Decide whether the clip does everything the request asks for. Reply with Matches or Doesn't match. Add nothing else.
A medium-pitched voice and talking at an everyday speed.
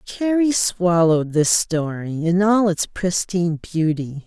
Doesn't match